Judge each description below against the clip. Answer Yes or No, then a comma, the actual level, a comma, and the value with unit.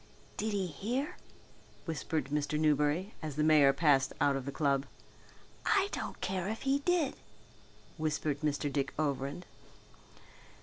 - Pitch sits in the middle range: Yes, medium, 155 Hz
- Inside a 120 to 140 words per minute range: Yes, slow, 135 wpm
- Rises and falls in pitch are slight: No, average, 5.3 semitones